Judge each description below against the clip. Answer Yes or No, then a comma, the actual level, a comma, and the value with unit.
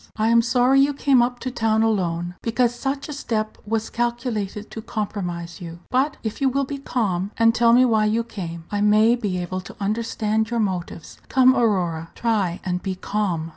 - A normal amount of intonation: Yes, average, 4.2 semitones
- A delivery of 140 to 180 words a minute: No, average, 195 wpm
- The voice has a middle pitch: No, high, 220 Hz